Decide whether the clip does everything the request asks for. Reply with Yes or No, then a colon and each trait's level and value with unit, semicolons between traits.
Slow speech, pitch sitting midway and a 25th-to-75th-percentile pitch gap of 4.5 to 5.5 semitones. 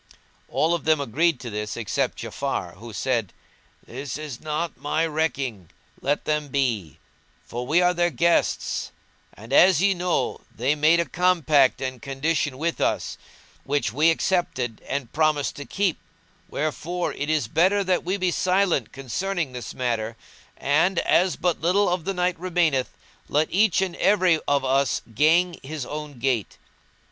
No: average, 155 wpm; medium, 155 Hz; average, 4.9 semitones